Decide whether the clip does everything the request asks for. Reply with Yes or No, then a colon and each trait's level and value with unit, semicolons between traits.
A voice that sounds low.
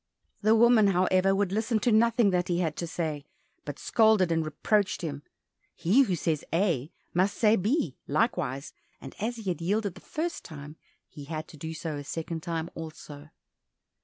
No: medium, 175 Hz